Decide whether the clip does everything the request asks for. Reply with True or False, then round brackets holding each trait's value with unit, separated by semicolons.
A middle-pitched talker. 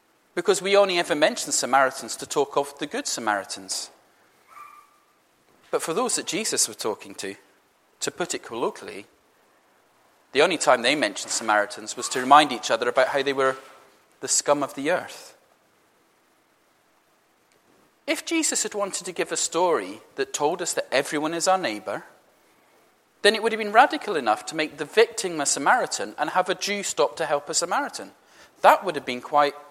True (170 Hz)